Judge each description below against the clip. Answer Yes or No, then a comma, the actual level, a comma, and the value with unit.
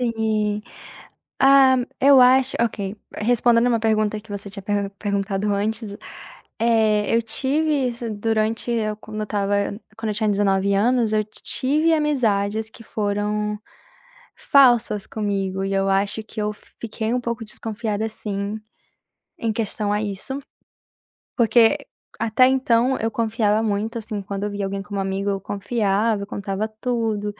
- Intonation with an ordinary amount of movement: No, narrow, 2.3 semitones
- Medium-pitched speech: No, high, 215 Hz